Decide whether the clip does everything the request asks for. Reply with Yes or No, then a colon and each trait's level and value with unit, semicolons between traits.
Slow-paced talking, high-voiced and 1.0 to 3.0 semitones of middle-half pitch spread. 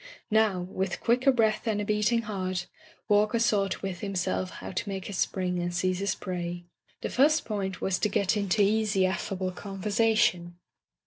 No: average, 170 wpm; high, 195 Hz; narrow, 2.6 semitones